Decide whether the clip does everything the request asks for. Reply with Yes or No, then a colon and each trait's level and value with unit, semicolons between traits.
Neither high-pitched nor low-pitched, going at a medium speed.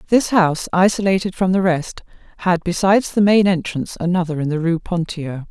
Yes: medium, 180 Hz; average, 175 wpm